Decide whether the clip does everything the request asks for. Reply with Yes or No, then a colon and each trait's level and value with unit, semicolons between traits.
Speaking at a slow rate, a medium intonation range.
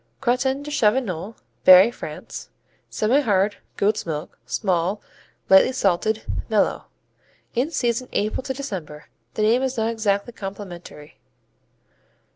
Yes: slow, 110 wpm; average, 4.5 semitones